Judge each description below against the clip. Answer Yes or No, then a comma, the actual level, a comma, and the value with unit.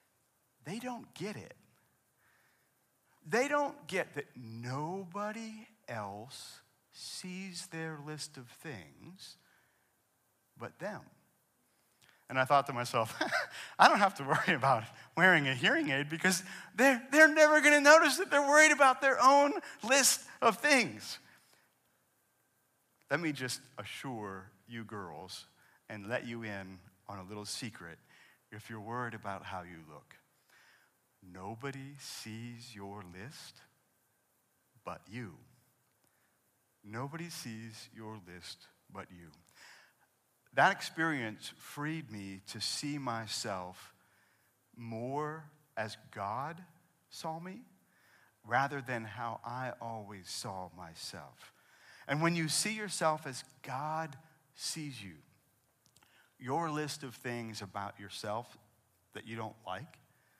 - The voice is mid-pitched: No, low, 125 Hz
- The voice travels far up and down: Yes, wide, 7.2 semitones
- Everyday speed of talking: No, slow, 120 wpm